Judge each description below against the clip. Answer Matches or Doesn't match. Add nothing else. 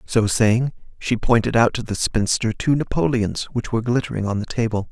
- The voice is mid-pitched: Doesn't match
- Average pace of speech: Matches